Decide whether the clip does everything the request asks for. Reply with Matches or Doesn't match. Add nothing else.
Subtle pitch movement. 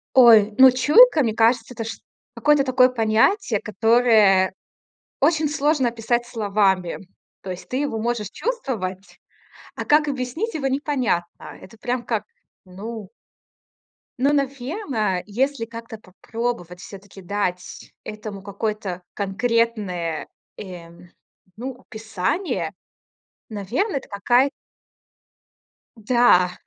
Doesn't match